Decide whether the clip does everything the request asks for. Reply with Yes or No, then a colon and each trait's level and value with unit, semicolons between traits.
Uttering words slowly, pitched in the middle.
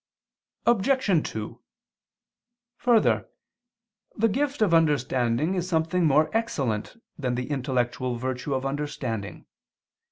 Yes: slow, 100 wpm; medium, 145 Hz